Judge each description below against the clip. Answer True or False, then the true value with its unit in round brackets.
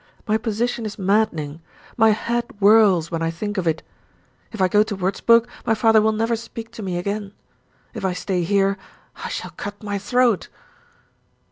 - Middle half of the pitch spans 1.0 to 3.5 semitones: True (2.8 semitones)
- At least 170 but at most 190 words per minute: True (175 wpm)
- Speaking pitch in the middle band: False (205 Hz)